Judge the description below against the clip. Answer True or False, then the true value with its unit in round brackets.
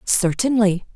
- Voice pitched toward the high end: True (205 Hz)